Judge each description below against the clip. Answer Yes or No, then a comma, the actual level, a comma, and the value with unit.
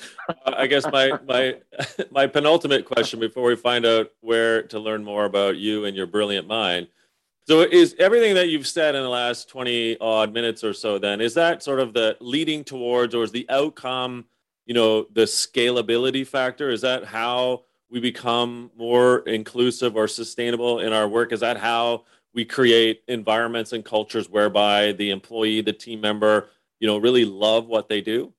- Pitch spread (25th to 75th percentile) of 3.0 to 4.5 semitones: No, narrow, 2.4 semitones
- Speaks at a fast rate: No, average, 180 wpm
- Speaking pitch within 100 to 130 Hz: Yes, low, 115 Hz